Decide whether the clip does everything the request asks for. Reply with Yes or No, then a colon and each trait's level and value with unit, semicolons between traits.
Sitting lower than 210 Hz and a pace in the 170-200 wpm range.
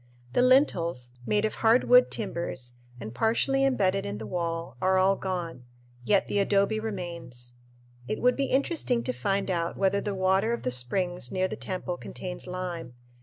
Yes: medium, 185 Hz; average, 175 wpm